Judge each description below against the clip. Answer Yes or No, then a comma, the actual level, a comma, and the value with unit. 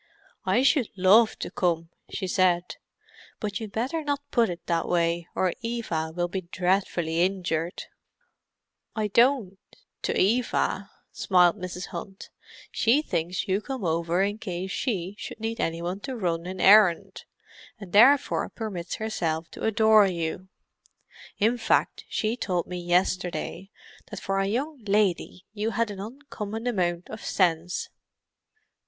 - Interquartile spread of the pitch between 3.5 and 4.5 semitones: Yes, average, 3.9 semitones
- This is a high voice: Yes, high, 195 Hz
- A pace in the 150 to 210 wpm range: No, average, 140 wpm